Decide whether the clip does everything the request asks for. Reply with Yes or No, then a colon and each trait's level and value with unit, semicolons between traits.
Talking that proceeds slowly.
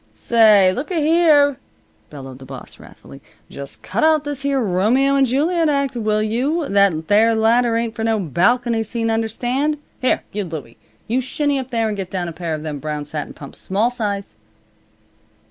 No: average, 180 wpm